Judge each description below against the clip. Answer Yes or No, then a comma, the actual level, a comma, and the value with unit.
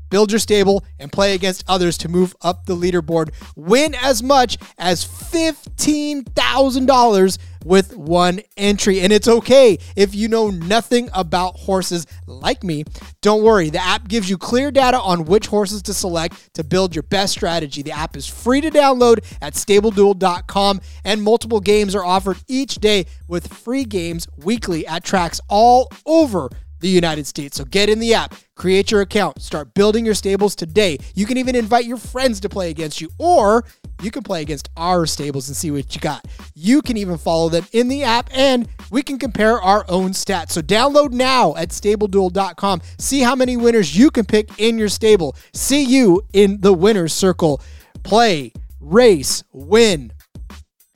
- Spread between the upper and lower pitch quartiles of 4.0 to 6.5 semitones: Yes, average, 5.1 semitones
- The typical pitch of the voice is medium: No, high, 200 Hz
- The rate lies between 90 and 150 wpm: No, average, 175 wpm